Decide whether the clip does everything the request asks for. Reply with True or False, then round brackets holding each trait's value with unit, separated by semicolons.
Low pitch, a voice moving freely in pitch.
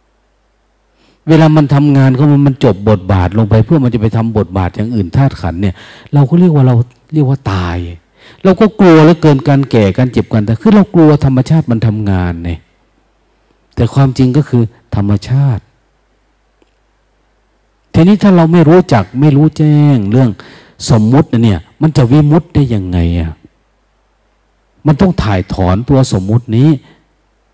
True (125 Hz; 6.0 semitones)